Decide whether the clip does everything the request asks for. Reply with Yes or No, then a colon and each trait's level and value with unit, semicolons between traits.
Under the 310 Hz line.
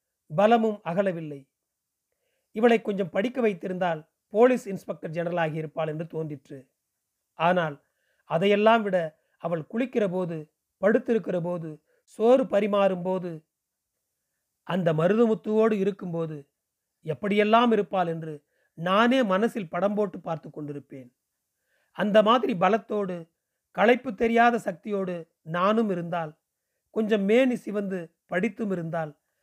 Yes: high, 190 Hz